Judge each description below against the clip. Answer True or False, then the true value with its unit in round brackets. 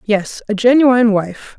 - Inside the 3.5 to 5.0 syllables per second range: True (4.2 syllables/s)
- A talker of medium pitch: False (220 Hz)